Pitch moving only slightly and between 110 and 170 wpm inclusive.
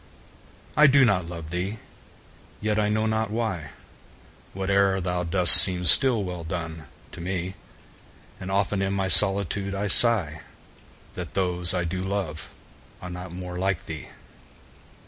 Yes: narrow, 2.3 semitones; average, 145 wpm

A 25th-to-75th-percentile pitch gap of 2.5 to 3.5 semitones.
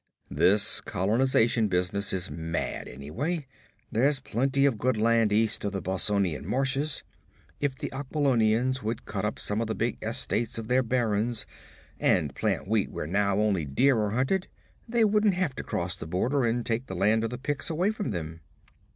No: average, 4.9 semitones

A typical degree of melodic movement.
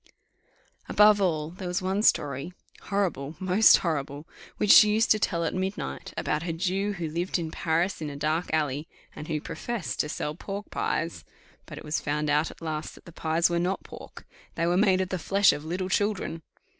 Yes: average, 3.7 semitones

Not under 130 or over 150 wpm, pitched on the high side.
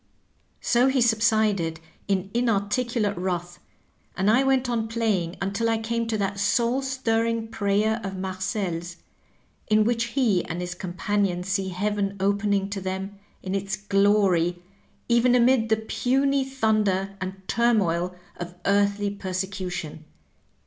Yes: slow, 135 wpm; high, 205 Hz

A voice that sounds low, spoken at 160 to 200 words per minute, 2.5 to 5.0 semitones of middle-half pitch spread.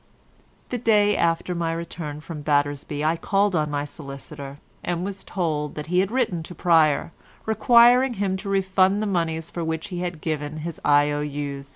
No: medium, 165 Hz; average, 175 wpm; average, 4.4 semitones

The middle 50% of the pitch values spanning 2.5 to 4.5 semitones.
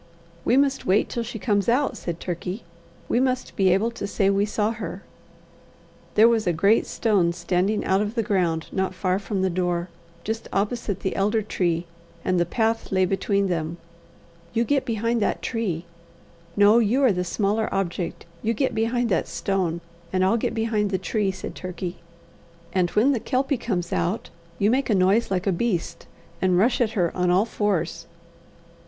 Yes: average, 3.7 semitones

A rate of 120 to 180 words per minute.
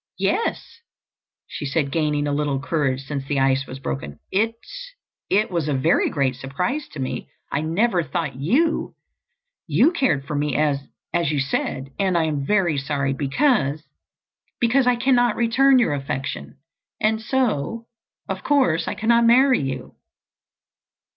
Yes: slow, 135 wpm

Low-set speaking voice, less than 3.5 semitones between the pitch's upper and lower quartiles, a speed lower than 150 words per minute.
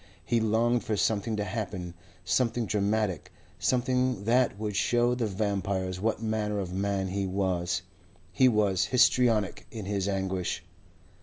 Yes: low, 105 Hz; average, 3.1 semitones; average, 140 wpm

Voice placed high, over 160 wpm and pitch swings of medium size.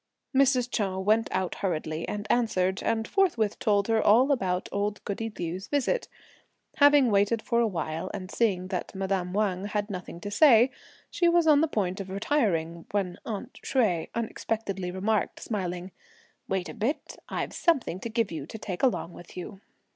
Yes: high, 205 Hz; average, 170 wpm; average, 4.0 semitones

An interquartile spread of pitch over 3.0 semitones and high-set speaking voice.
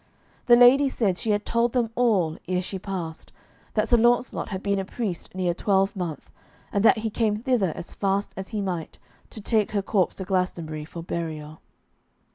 Yes: average, 3.9 semitones; high, 195 Hz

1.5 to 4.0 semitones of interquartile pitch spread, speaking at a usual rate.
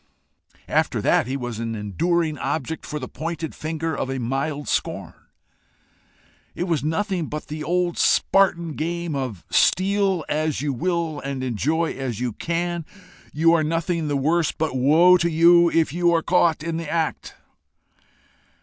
Yes: average, 3.4 semitones; average, 160 wpm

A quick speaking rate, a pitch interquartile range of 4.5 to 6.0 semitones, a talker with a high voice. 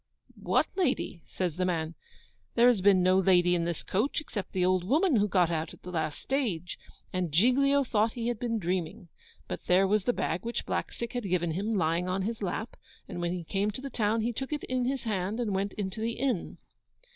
Yes: fast, 220 wpm; average, 4.8 semitones; high, 200 Hz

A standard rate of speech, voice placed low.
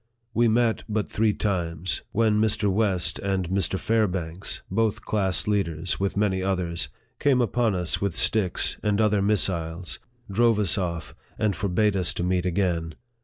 Yes: average, 155 wpm; low, 100 Hz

